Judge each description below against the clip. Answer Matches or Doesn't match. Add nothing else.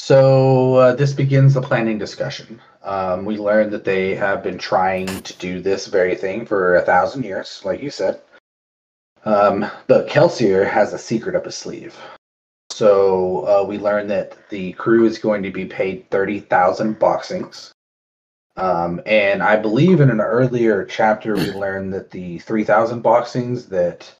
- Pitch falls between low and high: Doesn't match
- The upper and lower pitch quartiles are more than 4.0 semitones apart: Matches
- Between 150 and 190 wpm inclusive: Matches